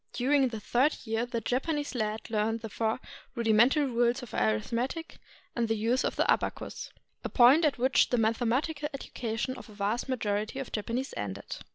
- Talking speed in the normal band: Yes, average, 175 wpm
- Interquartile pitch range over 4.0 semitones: No, average, 3.1 semitones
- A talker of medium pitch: No, high, 235 Hz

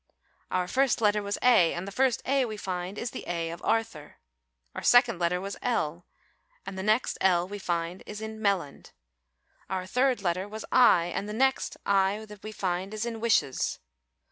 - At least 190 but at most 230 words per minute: Yes, average, 195 wpm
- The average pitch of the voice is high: Yes, high, 200 Hz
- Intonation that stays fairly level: No, average, 4.0 semitones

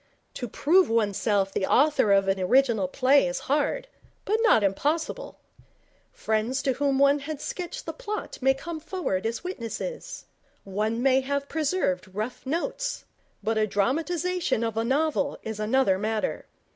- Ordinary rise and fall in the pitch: No, wide, 6.6 semitones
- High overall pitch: Yes, very high, 265 Hz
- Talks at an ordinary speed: Yes, average, 150 wpm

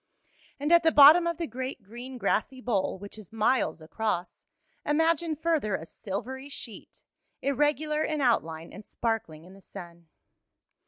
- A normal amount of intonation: No, wide, 7.0 semitones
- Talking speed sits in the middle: Yes, average, 150 wpm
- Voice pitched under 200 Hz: No, high, 245 Hz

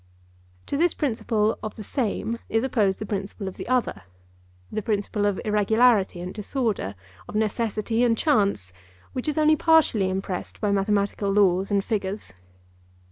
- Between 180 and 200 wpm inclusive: No, average, 145 wpm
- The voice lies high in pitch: Yes, high, 210 Hz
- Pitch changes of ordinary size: Yes, average, 3.0 semitones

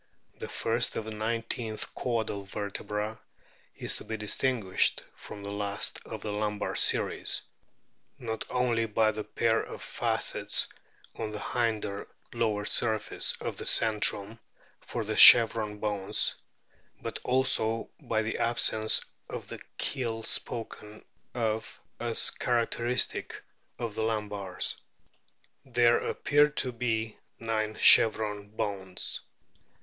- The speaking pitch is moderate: No, low, 110 Hz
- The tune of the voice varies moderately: No, narrow, 1.7 semitones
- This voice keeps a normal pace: No, slow, 120 wpm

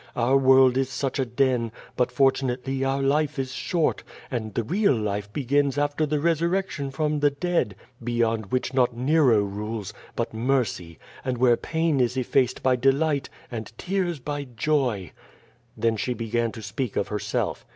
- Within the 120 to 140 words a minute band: No, average, 160 wpm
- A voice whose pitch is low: Yes, low, 130 Hz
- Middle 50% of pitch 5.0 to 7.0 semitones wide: No, average, 3.7 semitones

